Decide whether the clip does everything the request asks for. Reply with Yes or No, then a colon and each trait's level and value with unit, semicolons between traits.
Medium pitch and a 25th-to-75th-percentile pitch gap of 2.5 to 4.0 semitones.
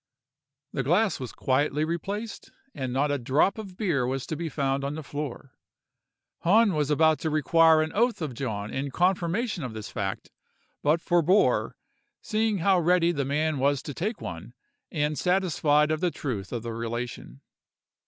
No: medium, 150 Hz; average, 4.8 semitones